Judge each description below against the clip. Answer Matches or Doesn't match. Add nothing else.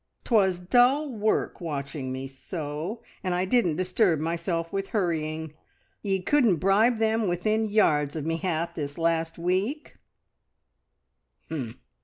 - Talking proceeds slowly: Matches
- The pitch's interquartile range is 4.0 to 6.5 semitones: Matches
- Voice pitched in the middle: Matches